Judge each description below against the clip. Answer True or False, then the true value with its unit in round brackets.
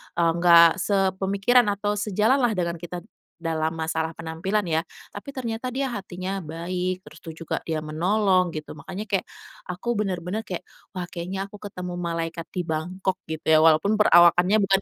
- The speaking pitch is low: False (180 Hz)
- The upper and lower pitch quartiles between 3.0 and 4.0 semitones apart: True (3.4 semitones)